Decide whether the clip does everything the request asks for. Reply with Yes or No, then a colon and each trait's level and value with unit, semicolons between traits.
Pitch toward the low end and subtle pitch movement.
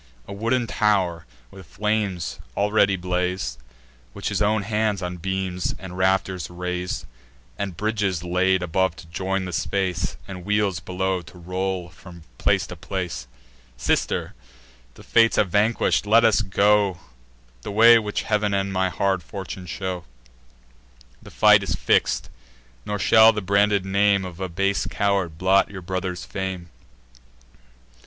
Yes: very low, 95 Hz; narrow, 2.3 semitones